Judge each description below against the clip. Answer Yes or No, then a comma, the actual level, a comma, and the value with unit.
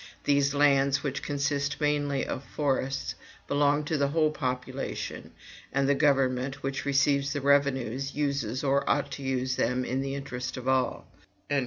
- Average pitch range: No, narrow, 1.3 semitones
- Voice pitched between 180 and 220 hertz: No, medium, 140 Hz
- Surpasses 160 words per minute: No, average, 155 wpm